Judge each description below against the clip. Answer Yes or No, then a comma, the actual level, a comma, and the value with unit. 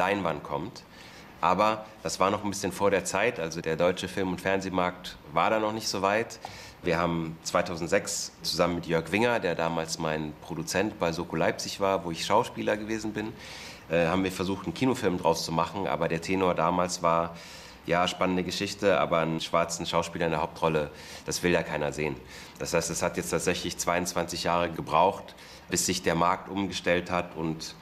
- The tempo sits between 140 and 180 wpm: No, fast, 190 wpm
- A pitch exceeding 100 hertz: No, very low, 85 Hz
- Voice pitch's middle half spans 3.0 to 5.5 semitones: No, narrow, 2.5 semitones